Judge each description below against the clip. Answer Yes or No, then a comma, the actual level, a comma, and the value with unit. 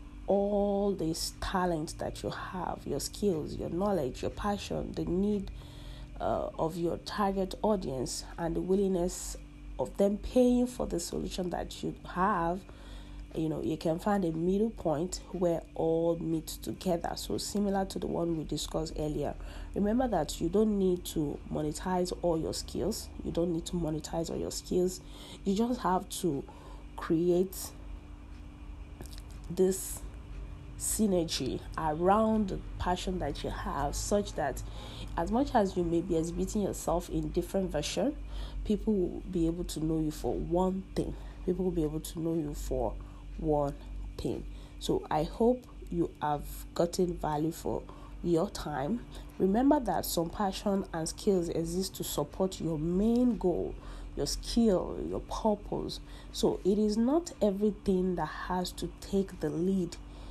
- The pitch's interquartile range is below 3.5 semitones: No, average, 3.8 semitones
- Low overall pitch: No, medium, 175 Hz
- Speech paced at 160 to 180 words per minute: No, average, 150 wpm